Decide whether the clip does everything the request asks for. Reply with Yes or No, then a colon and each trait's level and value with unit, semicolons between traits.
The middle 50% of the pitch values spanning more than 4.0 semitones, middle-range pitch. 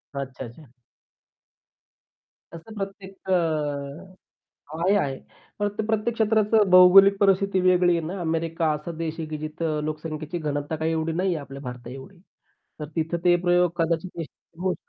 No: average, 3.7 semitones; medium, 165 Hz